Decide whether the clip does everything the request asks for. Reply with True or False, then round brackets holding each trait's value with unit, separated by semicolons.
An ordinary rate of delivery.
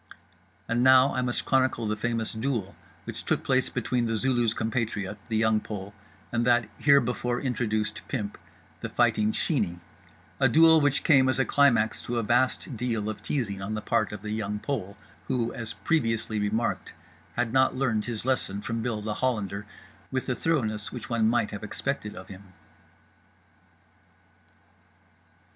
True (160 wpm)